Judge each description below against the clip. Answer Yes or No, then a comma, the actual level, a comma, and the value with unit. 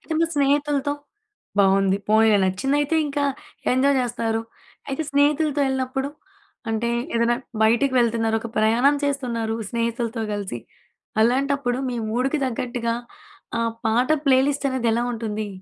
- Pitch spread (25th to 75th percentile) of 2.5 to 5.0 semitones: Yes, average, 3.6 semitones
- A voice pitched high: Yes, high, 245 Hz